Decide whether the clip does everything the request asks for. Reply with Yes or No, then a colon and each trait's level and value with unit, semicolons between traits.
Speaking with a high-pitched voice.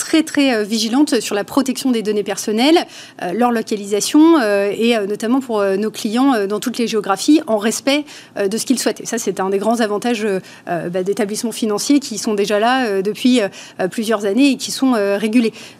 Yes: high, 225 Hz